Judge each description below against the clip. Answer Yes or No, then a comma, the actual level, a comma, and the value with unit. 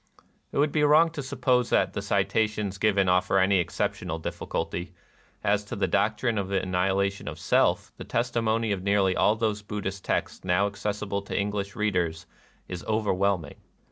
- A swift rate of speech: No, average, 170 wpm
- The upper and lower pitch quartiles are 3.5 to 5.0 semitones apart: No, narrow, 2.5 semitones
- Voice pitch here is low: Yes, low, 100 Hz